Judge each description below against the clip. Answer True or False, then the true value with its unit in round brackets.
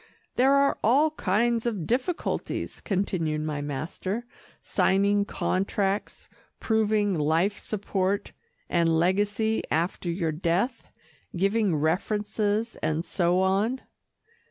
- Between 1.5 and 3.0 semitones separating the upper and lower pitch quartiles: False (4.3 semitones)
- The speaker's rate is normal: False (100 wpm)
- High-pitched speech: True (200 Hz)